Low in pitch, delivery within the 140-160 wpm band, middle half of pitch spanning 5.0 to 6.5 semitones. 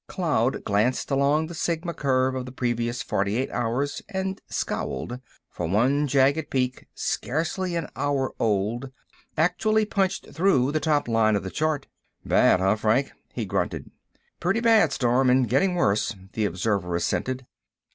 Yes: low, 130 Hz; average, 150 wpm; wide, 5.5 semitones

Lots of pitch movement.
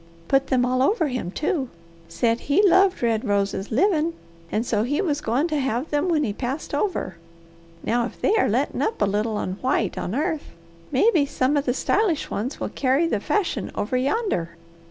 Yes: wide, 5.9 semitones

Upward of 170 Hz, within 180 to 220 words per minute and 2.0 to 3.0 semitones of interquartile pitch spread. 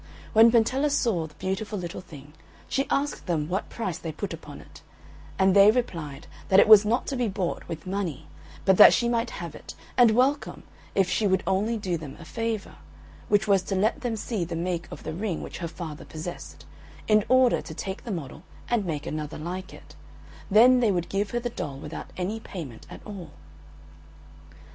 No: high, 190 Hz; average, 200 wpm; average, 5.0 semitones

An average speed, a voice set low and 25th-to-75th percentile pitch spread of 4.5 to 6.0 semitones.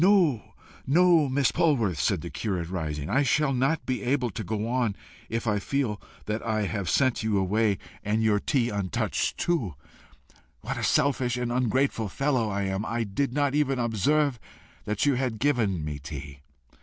Yes: average, 175 wpm; low, 115 Hz; average, 5.1 semitones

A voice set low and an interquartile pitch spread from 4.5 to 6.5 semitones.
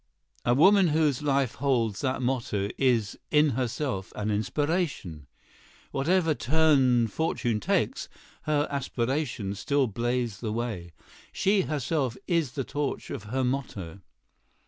Yes: low, 130 Hz; average, 4.8 semitones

